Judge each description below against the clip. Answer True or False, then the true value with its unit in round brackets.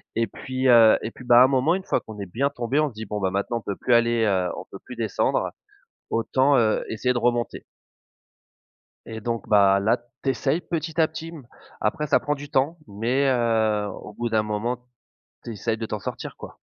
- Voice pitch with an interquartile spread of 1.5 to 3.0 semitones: False (3.5 semitones)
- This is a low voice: True (120 Hz)